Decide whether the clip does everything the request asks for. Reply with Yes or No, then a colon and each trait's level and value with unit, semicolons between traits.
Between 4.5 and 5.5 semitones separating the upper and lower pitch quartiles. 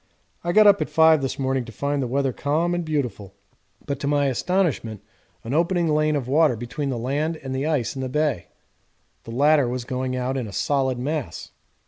No: average, 3.3 semitones